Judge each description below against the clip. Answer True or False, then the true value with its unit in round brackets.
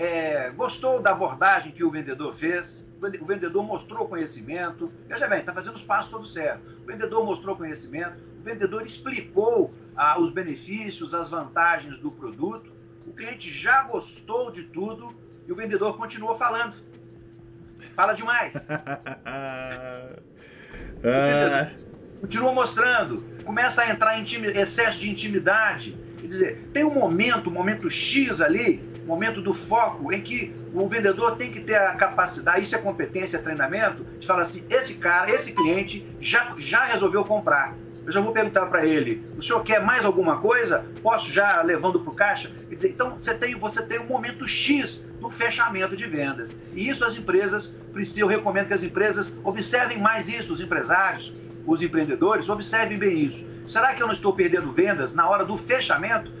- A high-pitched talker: True (200 Hz)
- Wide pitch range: True (6.6 semitones)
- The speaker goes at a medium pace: True (170 wpm)